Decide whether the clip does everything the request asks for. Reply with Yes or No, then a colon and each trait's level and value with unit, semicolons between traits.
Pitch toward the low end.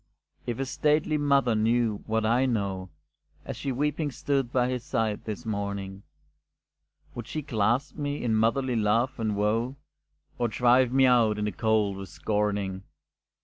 Yes: low, 115 Hz